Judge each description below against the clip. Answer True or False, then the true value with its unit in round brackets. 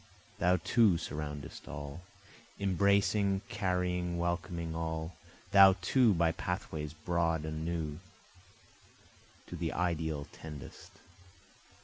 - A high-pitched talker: False (85 Hz)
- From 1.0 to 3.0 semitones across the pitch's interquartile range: True (2.5 semitones)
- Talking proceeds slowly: True (95 wpm)